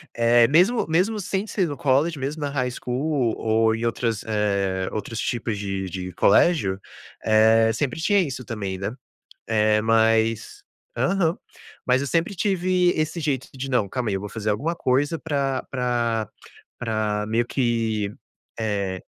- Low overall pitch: Yes, low, 120 Hz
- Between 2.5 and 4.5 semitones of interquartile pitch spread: No, average, 5.2 semitones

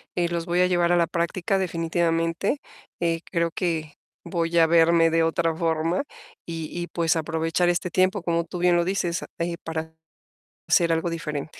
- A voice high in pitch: No, medium, 170 Hz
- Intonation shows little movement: Yes, narrow, 1.1 semitones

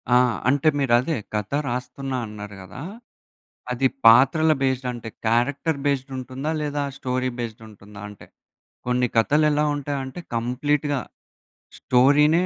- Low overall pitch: Yes, low, 130 Hz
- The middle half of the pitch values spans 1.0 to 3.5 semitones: Yes, average, 3.2 semitones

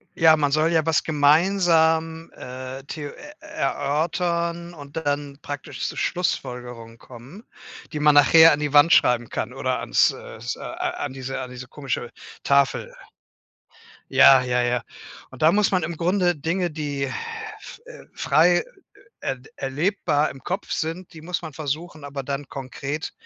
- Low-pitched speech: No, medium, 150 Hz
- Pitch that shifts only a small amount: No, average, 3.7 semitones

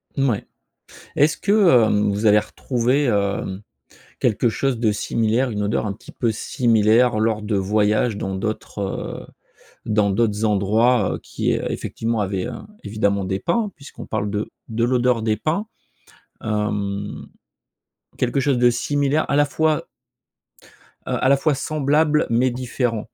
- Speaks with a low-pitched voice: Yes, low, 115 Hz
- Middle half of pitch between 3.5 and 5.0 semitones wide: Yes, average, 3.9 semitones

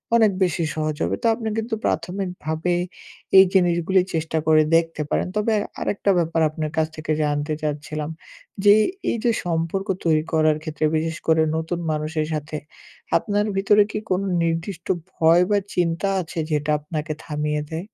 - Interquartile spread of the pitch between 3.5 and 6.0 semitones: No, average, 3.1 semitones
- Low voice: No, medium, 165 Hz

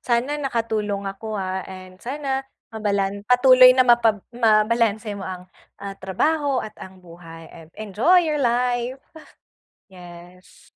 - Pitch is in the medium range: No, high, 215 Hz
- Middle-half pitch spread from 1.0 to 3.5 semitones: No, average, 4.8 semitones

